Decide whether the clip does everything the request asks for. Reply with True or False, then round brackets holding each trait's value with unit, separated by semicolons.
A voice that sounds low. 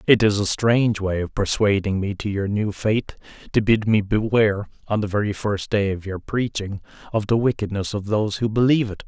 True (105 Hz)